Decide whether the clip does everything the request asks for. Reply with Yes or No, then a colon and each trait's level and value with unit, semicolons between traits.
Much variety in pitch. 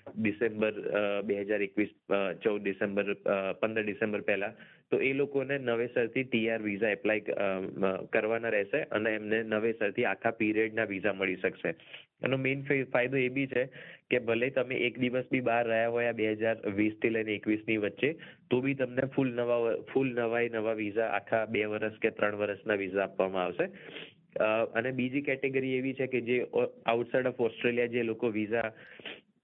No: average, 2.8 semitones